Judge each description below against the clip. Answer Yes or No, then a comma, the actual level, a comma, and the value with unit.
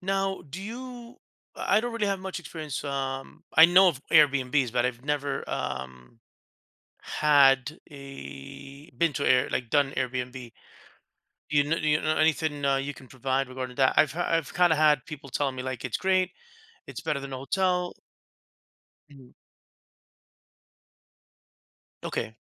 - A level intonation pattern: No, average, 4.2 semitones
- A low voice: No, medium, 145 Hz